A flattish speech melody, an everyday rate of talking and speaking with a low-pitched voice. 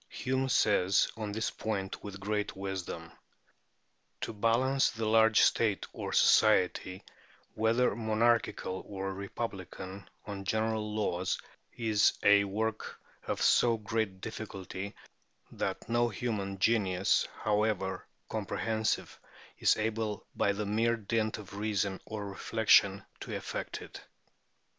No: narrow, 2.3 semitones; slow, 115 wpm; low, 105 Hz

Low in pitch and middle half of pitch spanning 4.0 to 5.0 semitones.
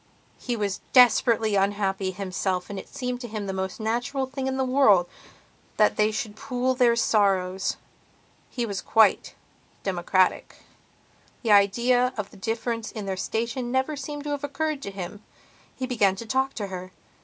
No: high, 220 Hz; average, 4.4 semitones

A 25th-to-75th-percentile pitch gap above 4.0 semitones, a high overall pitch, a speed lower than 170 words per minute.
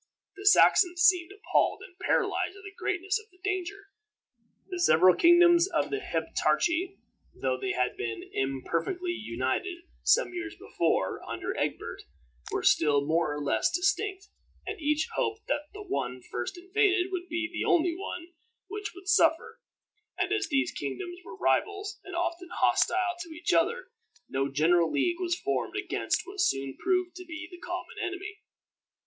Yes: average, 4.7 semitones; very high, 355 Hz; average, 160 wpm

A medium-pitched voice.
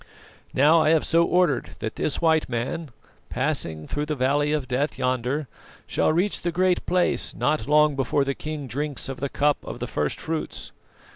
Yes: medium, 150 Hz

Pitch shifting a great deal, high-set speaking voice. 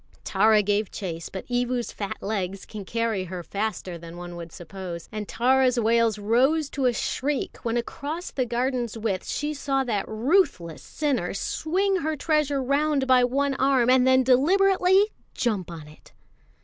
Yes: wide, 5.7 semitones; high, 240 Hz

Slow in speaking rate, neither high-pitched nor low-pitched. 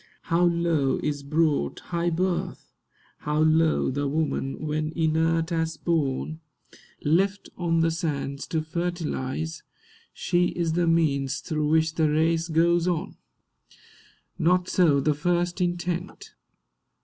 Yes: slow, 125 wpm; medium, 160 Hz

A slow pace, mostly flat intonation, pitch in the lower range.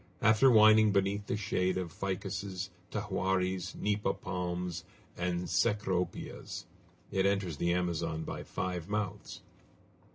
Yes: slow, 110 wpm; narrow, 2.2 semitones; very low, 95 Hz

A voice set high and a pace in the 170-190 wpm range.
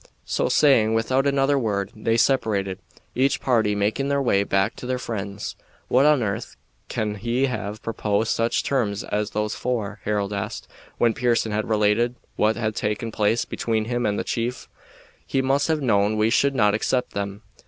No: low, 110 Hz; average, 175 wpm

